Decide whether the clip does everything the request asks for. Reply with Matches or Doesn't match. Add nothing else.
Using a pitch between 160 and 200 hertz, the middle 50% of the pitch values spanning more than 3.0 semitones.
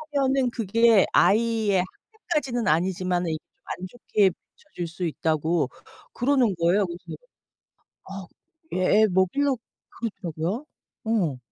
Matches